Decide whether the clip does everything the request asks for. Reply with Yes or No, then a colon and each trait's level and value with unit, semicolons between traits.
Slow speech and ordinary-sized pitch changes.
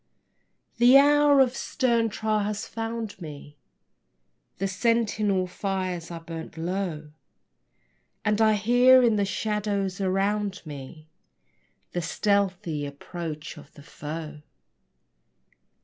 Yes: slow, 105 wpm; average, 4.9 semitones